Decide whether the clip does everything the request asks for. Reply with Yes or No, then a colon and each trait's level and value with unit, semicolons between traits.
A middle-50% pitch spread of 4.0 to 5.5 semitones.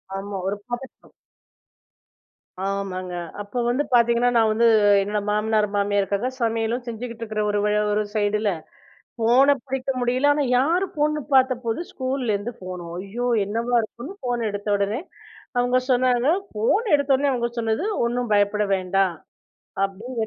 No: average, 3.4 semitones